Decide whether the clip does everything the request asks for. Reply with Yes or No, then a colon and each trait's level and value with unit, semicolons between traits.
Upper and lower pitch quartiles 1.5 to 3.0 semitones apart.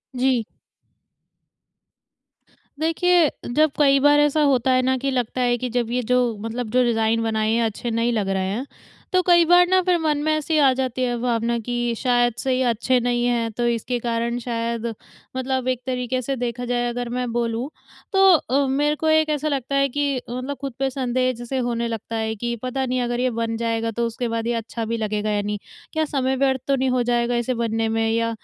Yes: narrow, 2.5 semitones